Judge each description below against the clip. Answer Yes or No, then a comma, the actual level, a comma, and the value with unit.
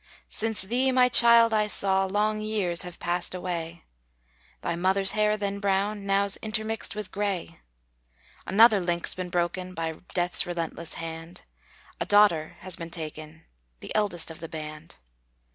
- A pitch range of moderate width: Yes, average, 3.8 semitones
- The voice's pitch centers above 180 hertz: Yes, high, 190 Hz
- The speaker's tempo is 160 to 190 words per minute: No, average, 145 wpm